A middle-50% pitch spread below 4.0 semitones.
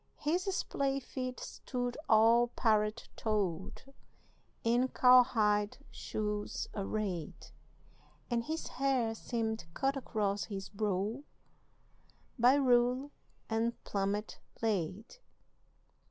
Yes: average, 3.3 semitones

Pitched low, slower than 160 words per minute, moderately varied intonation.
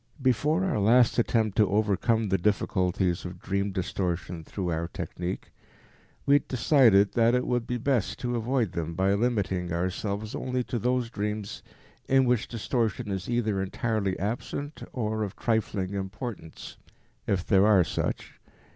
Yes: low, 105 Hz; average, 150 wpm; average, 4.1 semitones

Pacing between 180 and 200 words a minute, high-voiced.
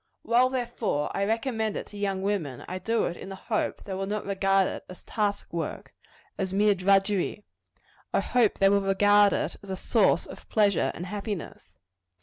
Yes: average, 190 wpm; high, 200 Hz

